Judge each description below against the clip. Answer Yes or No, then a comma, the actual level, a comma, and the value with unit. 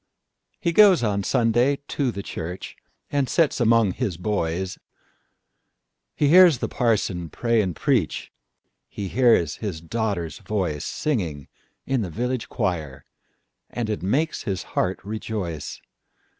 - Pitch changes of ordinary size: No, wide, 5.8 semitones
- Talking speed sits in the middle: No, slow, 110 wpm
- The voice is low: Yes, low, 105 Hz